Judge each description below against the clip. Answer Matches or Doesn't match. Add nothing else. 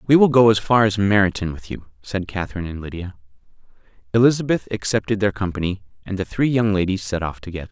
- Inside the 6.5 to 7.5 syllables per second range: Matches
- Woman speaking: Doesn't match